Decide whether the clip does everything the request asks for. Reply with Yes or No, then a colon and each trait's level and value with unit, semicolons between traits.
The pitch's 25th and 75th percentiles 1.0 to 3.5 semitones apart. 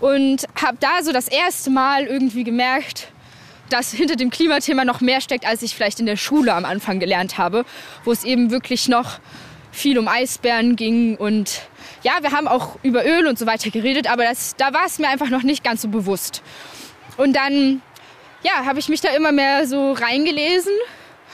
Yes: average, 3.2 semitones